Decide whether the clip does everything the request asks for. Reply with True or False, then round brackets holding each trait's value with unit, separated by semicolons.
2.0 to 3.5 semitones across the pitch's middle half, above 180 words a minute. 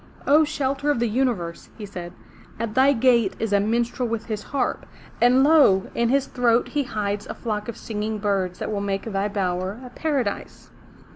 False (4.2 semitones; 190 wpm)